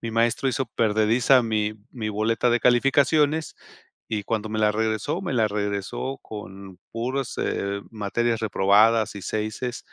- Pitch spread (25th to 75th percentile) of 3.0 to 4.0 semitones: No, narrow, 2.6 semitones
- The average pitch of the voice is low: Yes, low, 110 Hz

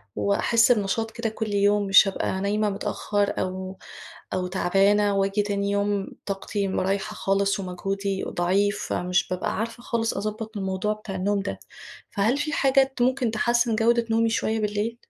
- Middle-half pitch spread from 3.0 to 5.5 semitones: No, narrow, 2.4 semitones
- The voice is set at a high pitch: Yes, high, 205 Hz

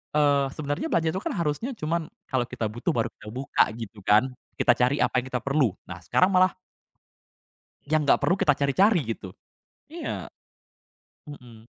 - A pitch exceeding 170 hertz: No, medium, 140 Hz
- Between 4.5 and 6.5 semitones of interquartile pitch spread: Yes, average, 5.0 semitones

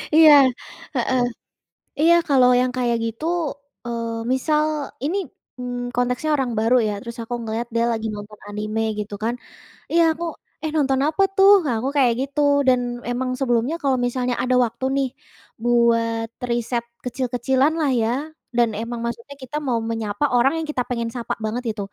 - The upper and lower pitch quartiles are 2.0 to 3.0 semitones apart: Yes, narrow, 2.6 semitones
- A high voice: Yes, high, 245 Hz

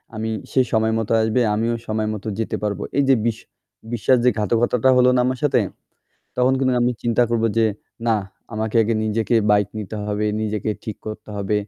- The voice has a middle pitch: No, low, 110 Hz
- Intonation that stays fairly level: Yes, narrow, 2.1 semitones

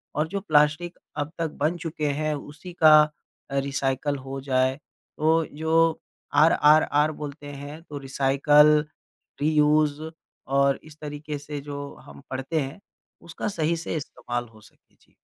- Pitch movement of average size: No, narrow, 2.0 semitones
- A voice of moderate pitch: Yes, medium, 150 Hz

